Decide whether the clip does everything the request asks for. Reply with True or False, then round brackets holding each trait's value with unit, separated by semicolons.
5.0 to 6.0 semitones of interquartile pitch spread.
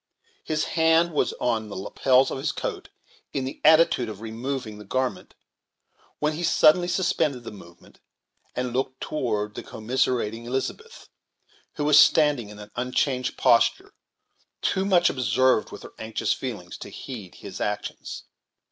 True (5.4 semitones)